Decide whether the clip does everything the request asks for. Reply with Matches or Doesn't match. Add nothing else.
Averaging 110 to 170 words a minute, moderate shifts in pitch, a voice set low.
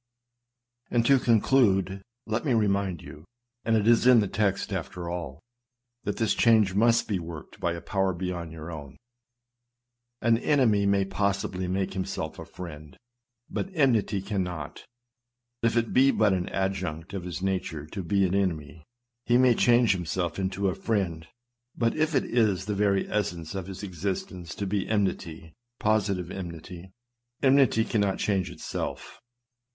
Matches